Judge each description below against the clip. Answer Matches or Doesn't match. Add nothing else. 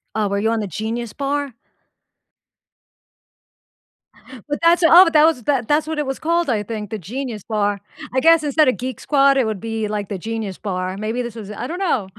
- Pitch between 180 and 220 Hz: Doesn't match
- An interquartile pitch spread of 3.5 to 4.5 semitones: Doesn't match